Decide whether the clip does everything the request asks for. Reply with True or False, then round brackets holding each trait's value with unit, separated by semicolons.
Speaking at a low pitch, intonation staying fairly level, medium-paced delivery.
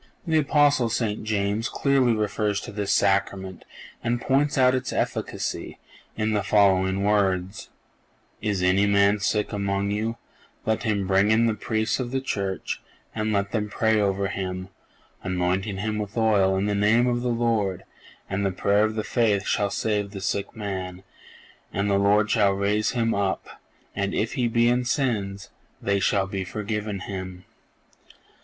True (105 Hz; 2.3 semitones; 160 wpm)